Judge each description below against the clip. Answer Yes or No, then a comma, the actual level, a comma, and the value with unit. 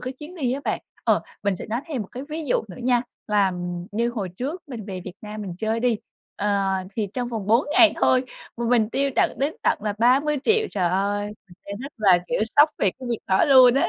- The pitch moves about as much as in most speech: Yes, average, 4.6 semitones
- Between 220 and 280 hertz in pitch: Yes, high, 235 Hz